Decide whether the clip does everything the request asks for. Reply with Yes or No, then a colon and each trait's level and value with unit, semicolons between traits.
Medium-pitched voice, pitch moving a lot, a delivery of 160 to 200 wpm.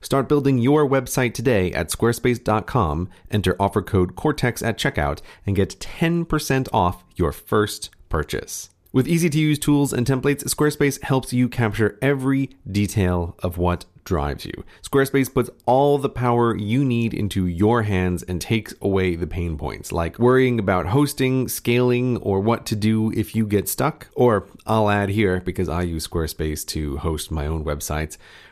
No: low, 110 Hz; wide, 6.5 semitones; average, 165 wpm